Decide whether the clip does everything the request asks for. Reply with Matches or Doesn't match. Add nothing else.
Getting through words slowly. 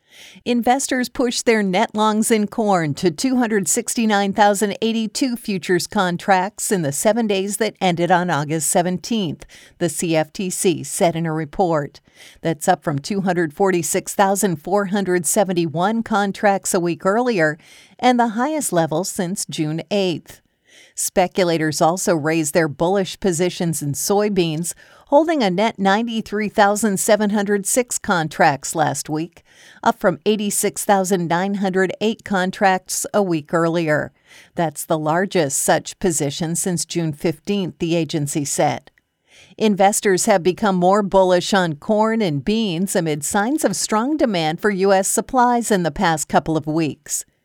Matches